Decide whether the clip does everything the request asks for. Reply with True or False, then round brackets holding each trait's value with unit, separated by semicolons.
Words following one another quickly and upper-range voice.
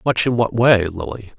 False (215 wpm; 105 Hz)